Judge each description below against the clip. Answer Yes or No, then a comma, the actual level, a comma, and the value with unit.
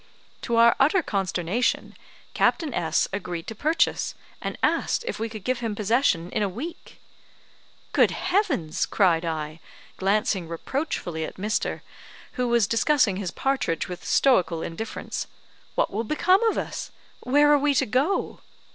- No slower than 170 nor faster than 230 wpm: No, average, 145 wpm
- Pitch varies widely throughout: Yes, wide, 7.3 semitones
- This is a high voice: Yes, high, 220 Hz